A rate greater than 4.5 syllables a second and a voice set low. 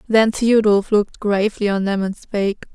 No: 5.1 syllables/s; high, 205 Hz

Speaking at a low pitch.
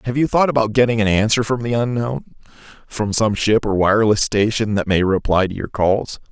Yes: low, 110 Hz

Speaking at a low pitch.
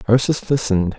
Yes: low, 115 Hz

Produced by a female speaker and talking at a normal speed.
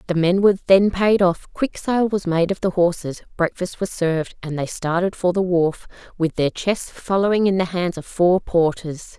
No: female; fast, 210 wpm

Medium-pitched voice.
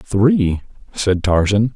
No: low, 105 Hz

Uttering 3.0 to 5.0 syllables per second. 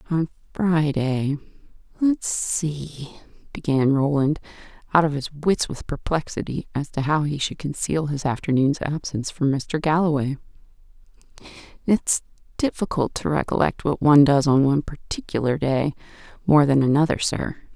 Yes: 4.9 syllables/s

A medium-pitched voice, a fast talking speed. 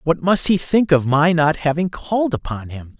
Yes: medium, 160 Hz; fast, 220 wpm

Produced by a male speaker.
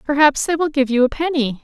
No: female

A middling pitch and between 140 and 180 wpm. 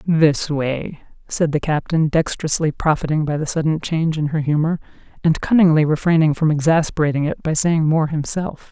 Yes: medium, 155 Hz; average, 165 wpm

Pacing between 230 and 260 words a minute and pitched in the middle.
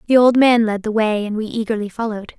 No: fast, 250 wpm; high, 220 Hz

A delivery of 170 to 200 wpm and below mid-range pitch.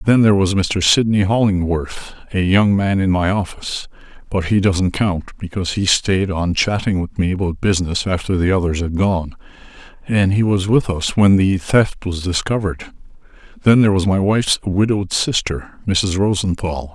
Yes: average, 175 wpm; very low, 95 Hz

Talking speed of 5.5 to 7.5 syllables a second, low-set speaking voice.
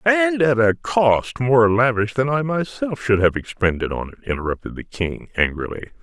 No: 4.9 syllables/s; low, 115 Hz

